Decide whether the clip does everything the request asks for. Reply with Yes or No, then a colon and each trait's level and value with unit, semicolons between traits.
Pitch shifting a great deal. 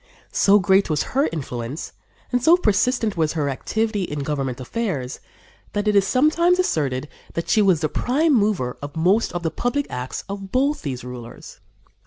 Yes: wide, 8.3 semitones